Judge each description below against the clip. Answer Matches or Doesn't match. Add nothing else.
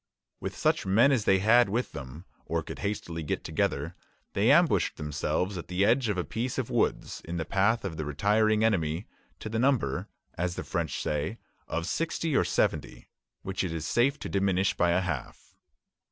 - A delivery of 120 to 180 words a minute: Doesn't match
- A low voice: Matches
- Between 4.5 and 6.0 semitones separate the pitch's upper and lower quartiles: Matches